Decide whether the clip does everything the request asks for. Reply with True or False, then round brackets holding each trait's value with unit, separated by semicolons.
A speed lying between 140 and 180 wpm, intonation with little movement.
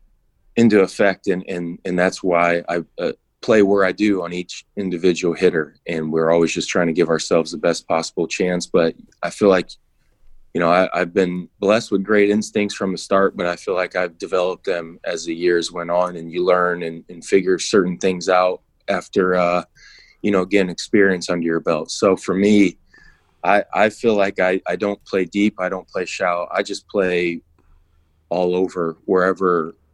False (195 wpm; 1.9 semitones)